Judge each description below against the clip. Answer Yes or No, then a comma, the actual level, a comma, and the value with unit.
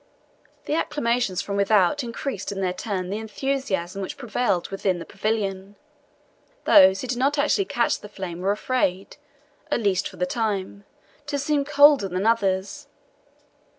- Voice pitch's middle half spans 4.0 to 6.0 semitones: Yes, average, 5.0 semitones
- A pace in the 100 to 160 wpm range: Yes, average, 150 wpm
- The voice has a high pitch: Yes, high, 205 Hz